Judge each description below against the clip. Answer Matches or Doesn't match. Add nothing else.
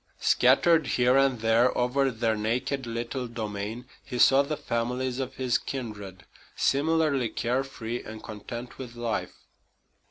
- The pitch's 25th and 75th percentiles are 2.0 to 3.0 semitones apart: Matches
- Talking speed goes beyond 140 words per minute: Doesn't match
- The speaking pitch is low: Matches